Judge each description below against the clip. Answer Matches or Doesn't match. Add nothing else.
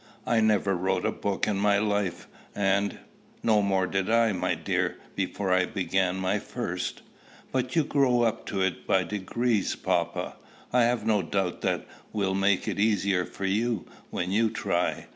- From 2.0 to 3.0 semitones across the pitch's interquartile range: Matches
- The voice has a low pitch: Matches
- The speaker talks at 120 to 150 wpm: Doesn't match